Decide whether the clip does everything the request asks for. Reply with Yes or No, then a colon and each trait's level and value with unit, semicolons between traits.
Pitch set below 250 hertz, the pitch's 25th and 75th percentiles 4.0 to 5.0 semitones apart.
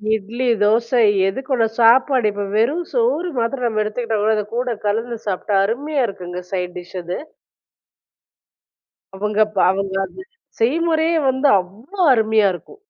Yes: high, 225 Hz; average, 4.4 semitones